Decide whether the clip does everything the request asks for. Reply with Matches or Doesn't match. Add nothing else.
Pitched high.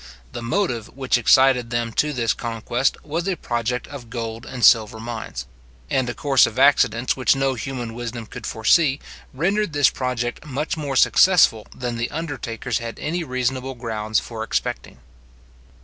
Doesn't match